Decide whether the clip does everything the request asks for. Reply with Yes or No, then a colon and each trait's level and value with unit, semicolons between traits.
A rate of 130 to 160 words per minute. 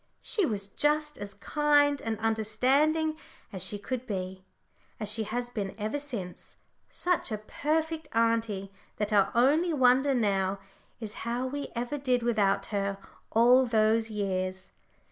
Yes: average, 145 wpm